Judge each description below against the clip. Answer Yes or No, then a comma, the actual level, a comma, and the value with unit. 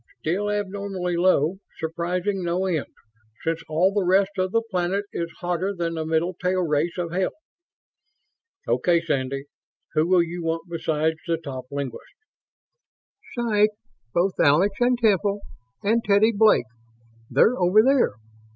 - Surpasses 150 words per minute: No, average, 140 wpm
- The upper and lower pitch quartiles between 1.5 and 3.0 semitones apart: No, average, 3.5 semitones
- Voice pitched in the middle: Yes, medium, 180 Hz